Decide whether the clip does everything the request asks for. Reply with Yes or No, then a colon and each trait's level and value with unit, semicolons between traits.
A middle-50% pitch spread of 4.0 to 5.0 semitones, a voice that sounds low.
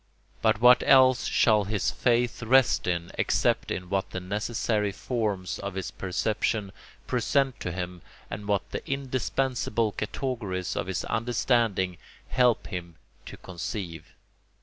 Yes: average, 4.7 semitones; low, 105 Hz